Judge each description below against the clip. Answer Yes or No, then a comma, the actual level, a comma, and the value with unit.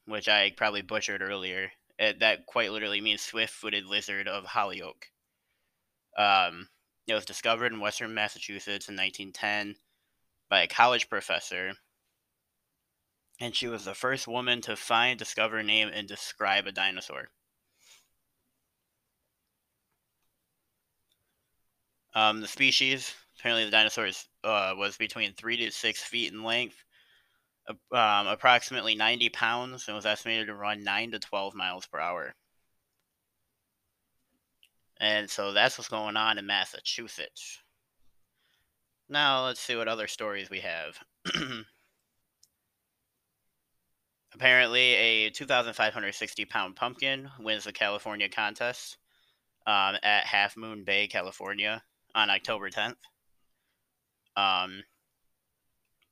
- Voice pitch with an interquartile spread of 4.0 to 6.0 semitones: No, narrow, 2.4 semitones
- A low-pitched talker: Yes, low, 110 Hz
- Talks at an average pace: No, slow, 115 wpm